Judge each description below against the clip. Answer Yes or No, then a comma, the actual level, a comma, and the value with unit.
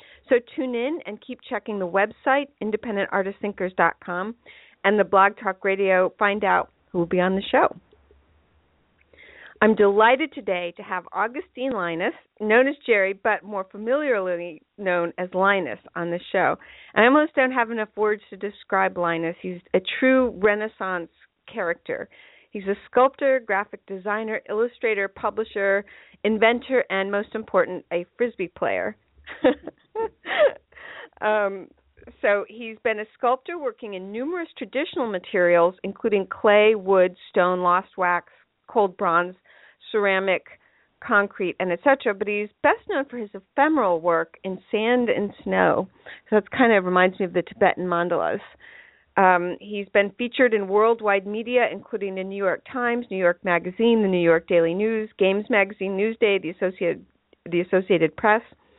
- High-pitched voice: Yes, high, 205 Hz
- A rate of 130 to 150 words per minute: Yes, average, 145 wpm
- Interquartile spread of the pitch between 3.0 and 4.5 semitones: Yes, average, 3.9 semitones